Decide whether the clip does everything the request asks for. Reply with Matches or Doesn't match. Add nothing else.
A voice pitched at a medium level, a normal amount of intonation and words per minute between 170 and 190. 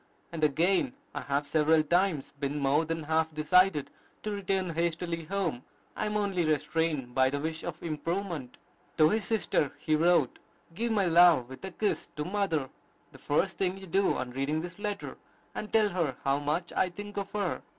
Matches